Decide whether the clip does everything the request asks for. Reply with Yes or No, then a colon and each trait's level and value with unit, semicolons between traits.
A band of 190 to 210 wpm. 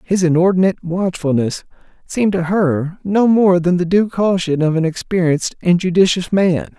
No: average, 160 wpm